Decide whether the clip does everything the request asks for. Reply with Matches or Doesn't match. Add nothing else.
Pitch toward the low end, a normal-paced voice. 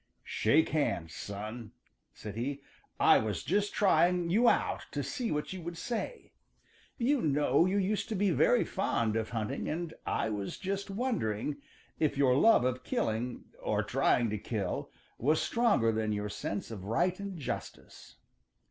Doesn't match